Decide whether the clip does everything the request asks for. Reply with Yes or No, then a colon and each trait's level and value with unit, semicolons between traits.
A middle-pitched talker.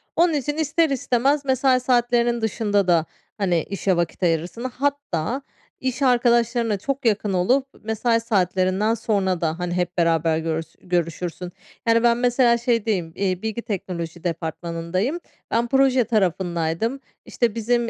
No: high, 220 Hz